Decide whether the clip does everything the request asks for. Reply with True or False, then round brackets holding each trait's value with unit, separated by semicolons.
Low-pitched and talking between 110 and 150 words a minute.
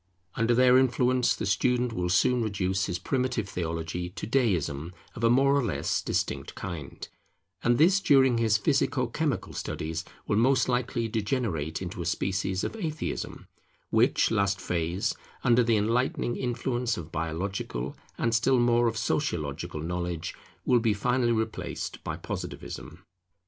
True (115 Hz; 145 wpm)